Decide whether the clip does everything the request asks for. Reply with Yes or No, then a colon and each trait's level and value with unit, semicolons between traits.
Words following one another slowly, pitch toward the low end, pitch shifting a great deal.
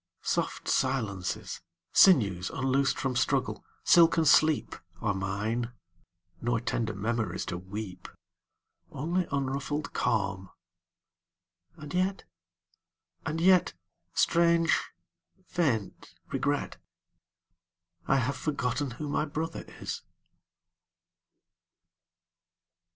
Yes: slow, 95 wpm; low, 125 Hz; wide, 7.3 semitones